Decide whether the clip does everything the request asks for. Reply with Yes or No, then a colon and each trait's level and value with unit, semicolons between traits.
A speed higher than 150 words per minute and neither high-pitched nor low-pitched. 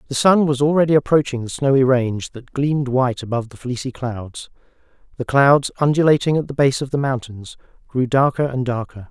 No: average, 185 wpm; low, 130 Hz